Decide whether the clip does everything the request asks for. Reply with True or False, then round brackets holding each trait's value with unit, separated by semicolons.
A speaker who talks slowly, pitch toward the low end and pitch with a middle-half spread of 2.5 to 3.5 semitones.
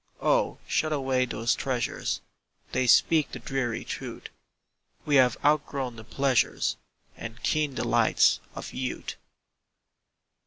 True (115 wpm; 130 Hz; 2.9 semitones)